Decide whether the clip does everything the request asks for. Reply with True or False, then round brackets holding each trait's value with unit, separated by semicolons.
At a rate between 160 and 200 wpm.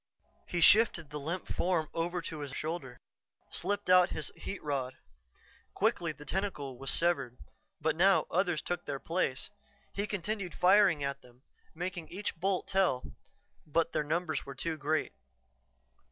False (150 wpm)